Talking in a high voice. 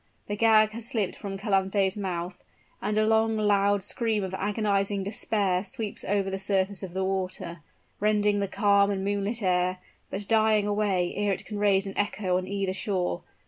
Yes: high, 200 Hz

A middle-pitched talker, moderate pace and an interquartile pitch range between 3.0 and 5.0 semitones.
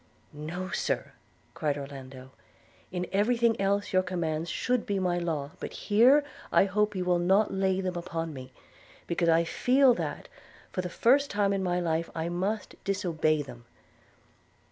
Yes: medium, 180 Hz; average, 165 wpm; average, 3.7 semitones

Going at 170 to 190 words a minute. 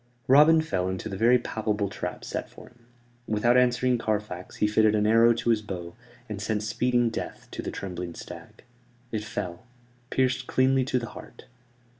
Yes: average, 175 wpm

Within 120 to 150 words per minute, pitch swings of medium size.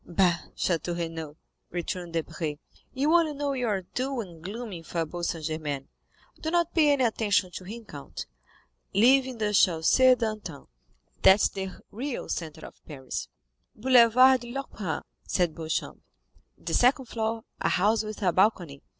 No: average, 140 wpm; wide, 6.9 semitones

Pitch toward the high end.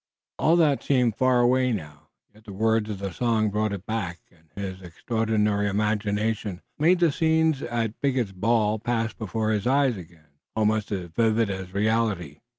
No: low, 110 Hz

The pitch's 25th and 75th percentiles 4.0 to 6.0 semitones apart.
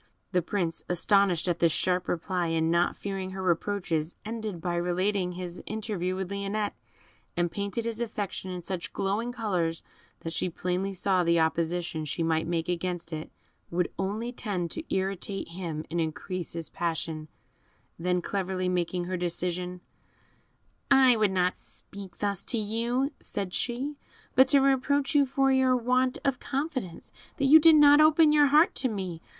Yes: average, 5.0 semitones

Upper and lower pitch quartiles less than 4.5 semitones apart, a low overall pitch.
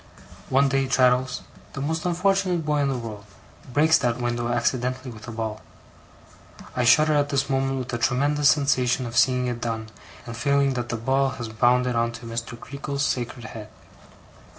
Yes: average, 2.9 semitones; low, 125 Hz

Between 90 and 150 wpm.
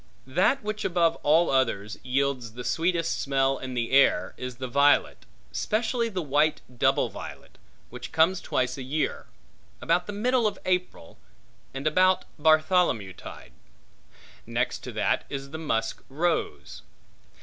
Yes: average, 140 wpm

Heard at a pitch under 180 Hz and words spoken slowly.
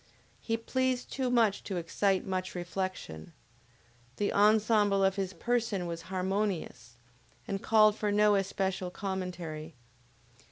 No: high, 195 Hz; slow, 120 wpm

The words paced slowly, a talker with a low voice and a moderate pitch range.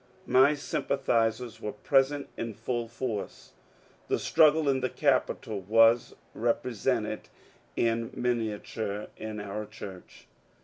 Yes: slow, 115 wpm; low, 115 Hz; average, 3.1 semitones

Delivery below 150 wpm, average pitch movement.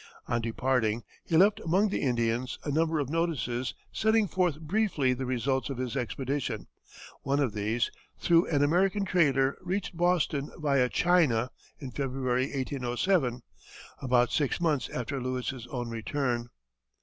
Yes: average, 140 wpm; average, 5.0 semitones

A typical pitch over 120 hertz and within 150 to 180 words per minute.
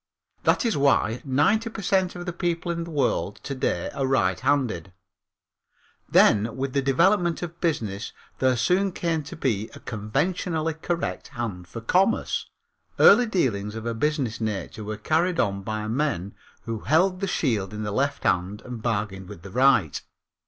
Yes: low, 135 Hz; average, 165 wpm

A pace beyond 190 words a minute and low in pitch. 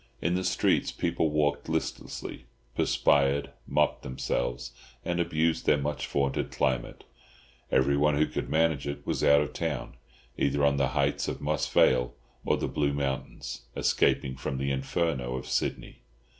No: average, 150 wpm; very low, 70 Hz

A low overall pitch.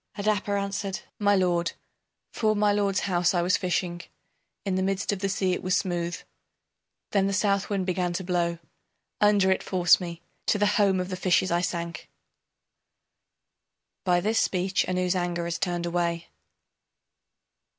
No: medium, 185 Hz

